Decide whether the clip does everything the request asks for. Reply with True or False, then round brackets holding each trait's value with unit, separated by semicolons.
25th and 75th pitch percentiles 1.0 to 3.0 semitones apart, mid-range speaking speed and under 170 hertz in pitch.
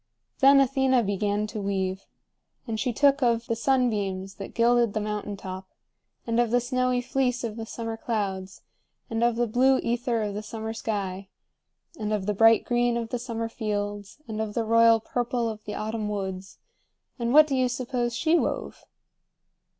False (2.7 semitones; 180 wpm; 225 Hz)